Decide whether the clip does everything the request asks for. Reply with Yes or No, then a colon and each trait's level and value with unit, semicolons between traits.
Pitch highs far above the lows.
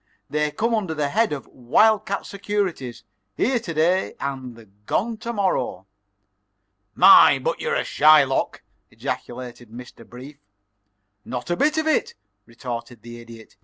Yes: wide, 8.7 semitones